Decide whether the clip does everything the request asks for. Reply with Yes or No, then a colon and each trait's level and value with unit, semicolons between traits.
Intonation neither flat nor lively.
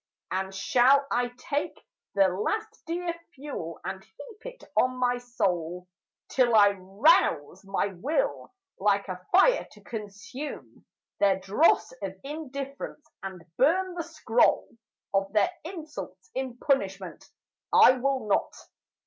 No: wide, 7.5 semitones